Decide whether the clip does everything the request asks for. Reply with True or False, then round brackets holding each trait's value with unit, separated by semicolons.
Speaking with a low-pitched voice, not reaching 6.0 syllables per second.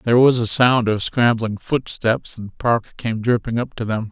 True (115 Hz; 4.4 syllables/s)